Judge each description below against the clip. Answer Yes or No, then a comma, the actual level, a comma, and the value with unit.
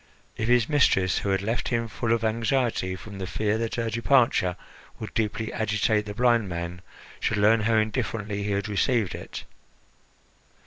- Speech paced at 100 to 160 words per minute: No, average, 170 wpm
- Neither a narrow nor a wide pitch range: No, narrow, 2.3 semitones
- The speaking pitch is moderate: No, low, 110 Hz